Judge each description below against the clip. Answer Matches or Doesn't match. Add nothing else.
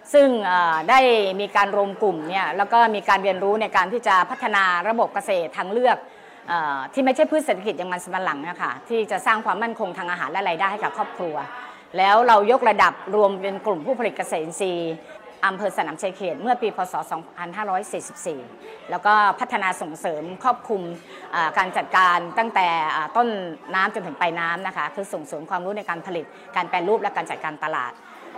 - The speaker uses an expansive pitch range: Doesn't match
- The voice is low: Doesn't match